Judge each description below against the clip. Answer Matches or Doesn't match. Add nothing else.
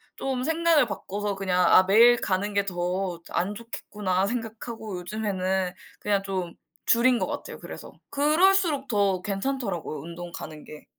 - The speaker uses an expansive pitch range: Doesn't match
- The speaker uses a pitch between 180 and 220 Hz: Matches